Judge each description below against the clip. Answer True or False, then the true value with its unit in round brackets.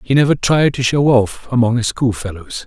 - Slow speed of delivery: False (205 wpm)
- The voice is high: False (125 Hz)